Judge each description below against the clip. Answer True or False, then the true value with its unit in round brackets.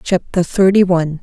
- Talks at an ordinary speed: True (145 wpm)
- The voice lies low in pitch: False (180 Hz)